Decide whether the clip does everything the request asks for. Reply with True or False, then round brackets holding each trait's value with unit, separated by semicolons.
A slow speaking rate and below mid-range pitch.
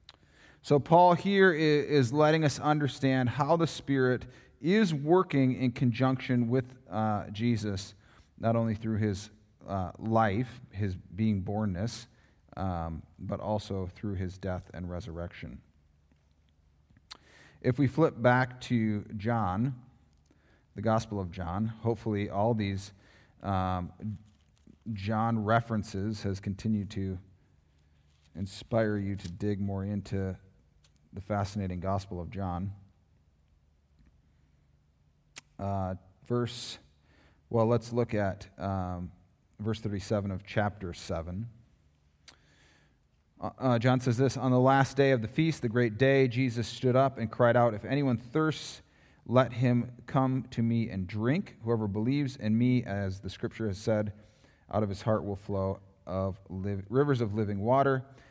True (130 wpm; 105 Hz)